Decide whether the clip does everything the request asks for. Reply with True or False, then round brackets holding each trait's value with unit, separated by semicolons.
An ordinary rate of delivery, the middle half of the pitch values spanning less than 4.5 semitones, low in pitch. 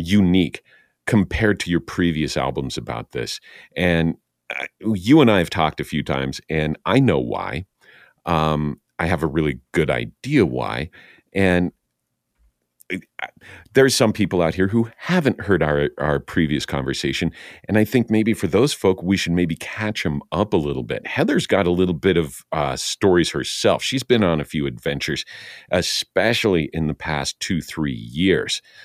False (165 wpm; 5.2 semitones; 85 Hz)